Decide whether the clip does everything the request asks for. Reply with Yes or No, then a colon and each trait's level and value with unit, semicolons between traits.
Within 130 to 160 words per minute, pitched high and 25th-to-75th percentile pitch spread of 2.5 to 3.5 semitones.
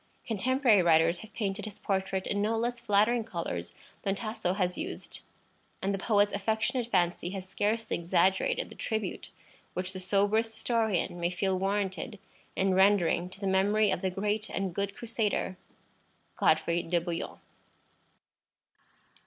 Yes: average, 145 wpm; high, 195 Hz; average, 2.9 semitones